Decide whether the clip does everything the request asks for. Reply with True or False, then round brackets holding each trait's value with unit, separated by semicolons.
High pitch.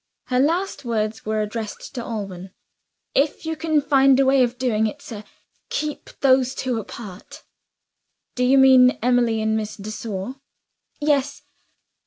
True (250 Hz)